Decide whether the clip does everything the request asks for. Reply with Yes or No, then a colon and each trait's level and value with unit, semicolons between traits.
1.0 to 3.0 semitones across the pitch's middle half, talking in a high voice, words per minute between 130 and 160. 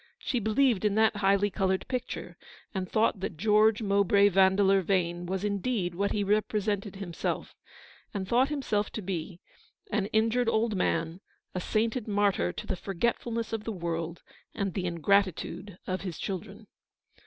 Yes: average, 2.7 semitones; high, 200 Hz; average, 155 wpm